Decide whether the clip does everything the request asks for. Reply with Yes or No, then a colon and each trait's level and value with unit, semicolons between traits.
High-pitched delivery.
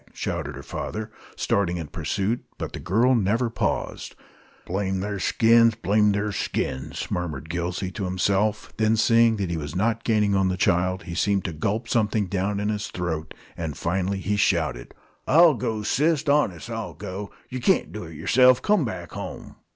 No: low, 100 Hz